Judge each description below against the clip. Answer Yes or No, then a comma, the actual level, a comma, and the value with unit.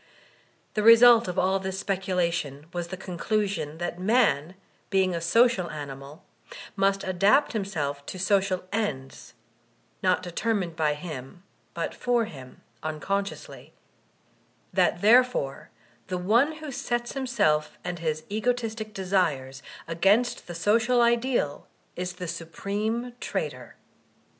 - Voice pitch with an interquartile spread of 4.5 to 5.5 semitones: Yes, average, 5.1 semitones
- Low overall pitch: No, high, 190 Hz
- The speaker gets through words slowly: Yes, slow, 125 wpm